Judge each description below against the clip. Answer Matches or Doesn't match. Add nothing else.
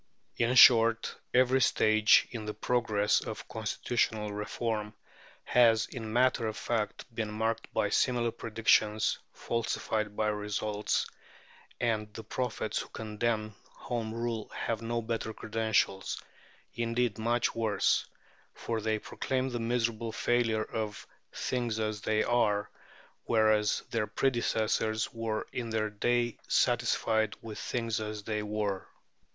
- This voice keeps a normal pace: Doesn't match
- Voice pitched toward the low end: Matches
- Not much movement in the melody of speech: Matches